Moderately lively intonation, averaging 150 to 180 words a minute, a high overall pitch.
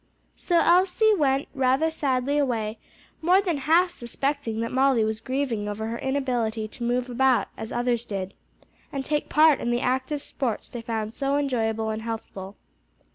Yes: average, 4.2 semitones; average, 165 wpm; very high, 255 Hz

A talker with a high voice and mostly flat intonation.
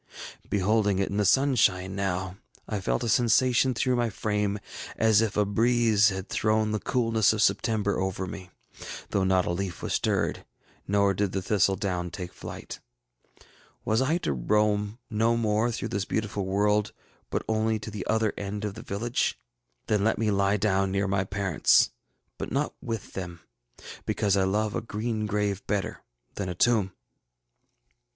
No: low, 105 Hz; narrow, 2.2 semitones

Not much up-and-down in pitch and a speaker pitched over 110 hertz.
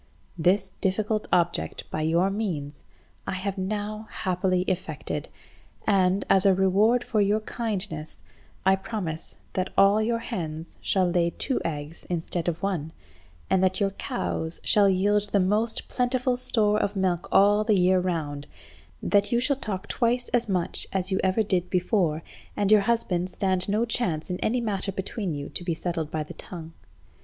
No: average, 3.3 semitones; high, 190 Hz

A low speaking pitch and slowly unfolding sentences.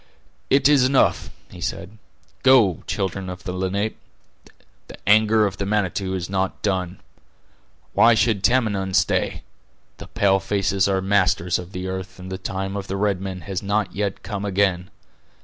No: very low, 95 Hz; average, 165 wpm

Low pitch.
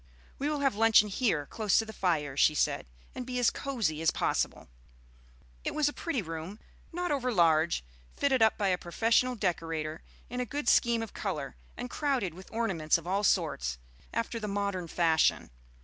No: high, 205 Hz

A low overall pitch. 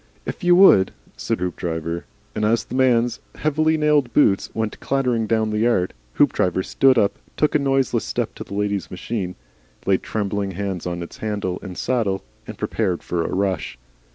Yes: low, 105 Hz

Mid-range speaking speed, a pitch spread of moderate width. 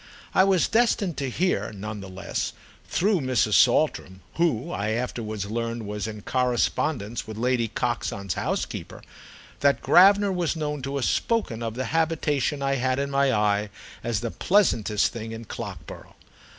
No: average, 150 wpm; wide, 6.1 semitones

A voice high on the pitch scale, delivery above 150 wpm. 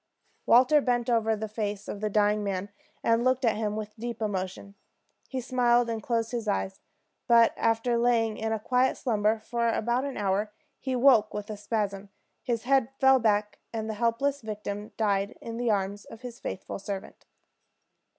Yes: high, 225 Hz; average, 180 wpm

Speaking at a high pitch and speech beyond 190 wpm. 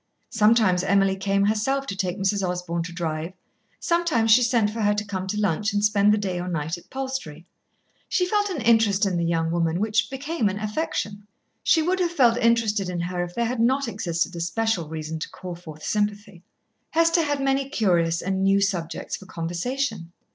Yes: high, 205 Hz; average, 200 wpm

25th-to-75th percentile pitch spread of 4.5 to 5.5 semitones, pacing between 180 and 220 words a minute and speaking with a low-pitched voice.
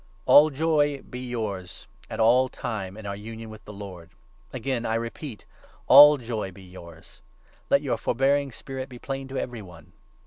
Yes: average, 4.9 semitones; average, 185 wpm; low, 115 Hz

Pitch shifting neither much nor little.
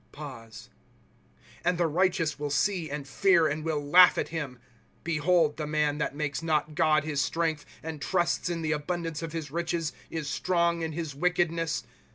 No: narrow, 2.3 semitones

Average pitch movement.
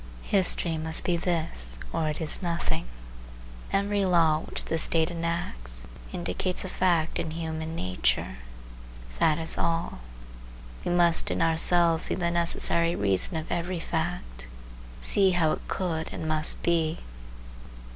No: narrow, 1.9 semitones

